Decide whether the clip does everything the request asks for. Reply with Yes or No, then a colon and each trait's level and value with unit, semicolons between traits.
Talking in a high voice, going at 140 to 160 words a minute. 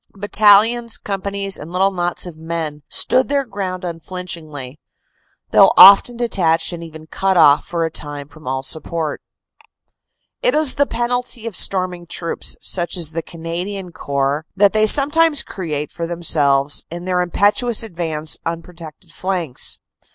No: medium, 175 Hz; average, 145 wpm